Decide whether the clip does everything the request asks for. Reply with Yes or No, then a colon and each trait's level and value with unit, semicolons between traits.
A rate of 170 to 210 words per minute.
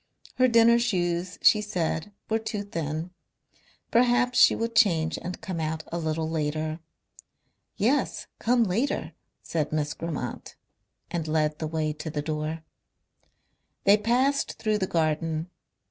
No: slow, 135 wpm